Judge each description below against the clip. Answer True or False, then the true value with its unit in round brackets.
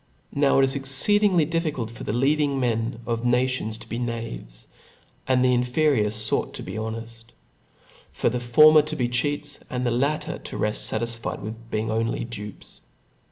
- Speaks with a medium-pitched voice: False (120 Hz)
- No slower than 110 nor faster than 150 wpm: False (175 wpm)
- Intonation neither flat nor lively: True (3.5 semitones)